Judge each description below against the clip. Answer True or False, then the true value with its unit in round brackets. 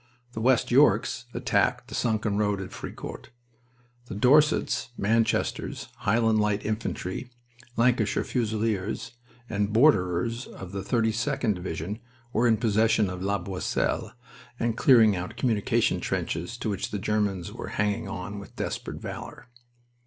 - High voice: False (110 Hz)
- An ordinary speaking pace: False (130 wpm)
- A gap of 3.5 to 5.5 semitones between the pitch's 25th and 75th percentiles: False (2.6 semitones)